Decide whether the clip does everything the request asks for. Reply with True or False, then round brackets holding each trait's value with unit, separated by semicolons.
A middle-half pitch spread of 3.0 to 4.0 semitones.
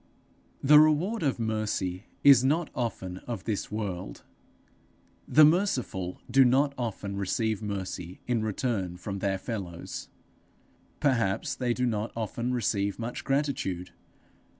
False (5.3 semitones)